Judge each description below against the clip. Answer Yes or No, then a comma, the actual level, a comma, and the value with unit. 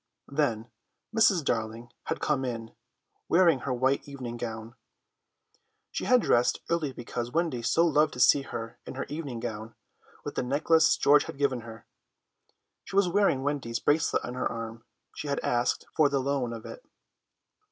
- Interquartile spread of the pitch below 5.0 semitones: Yes, average, 4.2 semitones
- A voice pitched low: Yes, low, 130 Hz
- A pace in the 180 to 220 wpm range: No, average, 165 wpm